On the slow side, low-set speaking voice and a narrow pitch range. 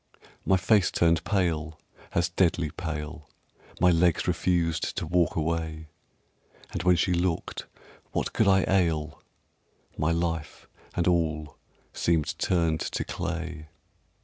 Yes: slow, 120 wpm; very low, 85 Hz; narrow, 2.0 semitones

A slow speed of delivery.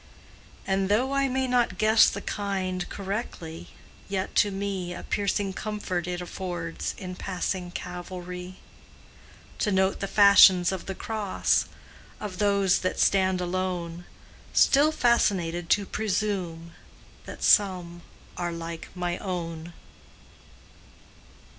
Yes: slow, 115 wpm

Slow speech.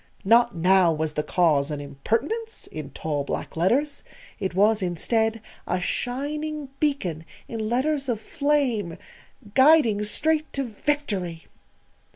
Yes: slow, 125 wpm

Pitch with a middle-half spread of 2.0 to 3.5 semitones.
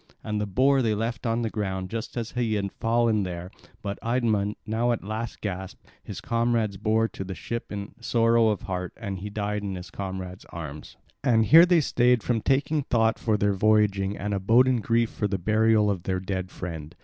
Yes: average, 3.0 semitones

